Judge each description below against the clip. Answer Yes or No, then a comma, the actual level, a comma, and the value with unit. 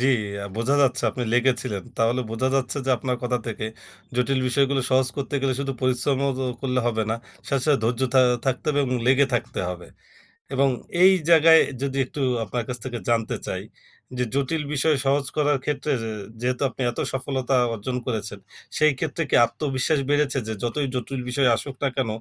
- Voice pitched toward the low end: Yes, low, 130 Hz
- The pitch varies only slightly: Yes, narrow, 2.2 semitones